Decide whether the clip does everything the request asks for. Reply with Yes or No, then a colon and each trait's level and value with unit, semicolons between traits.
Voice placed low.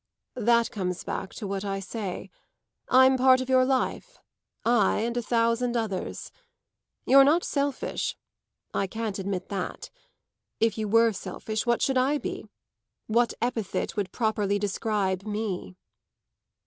No: high, 225 Hz